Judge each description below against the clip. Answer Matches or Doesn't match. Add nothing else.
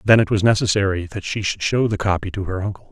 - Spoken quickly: Matches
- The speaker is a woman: Doesn't match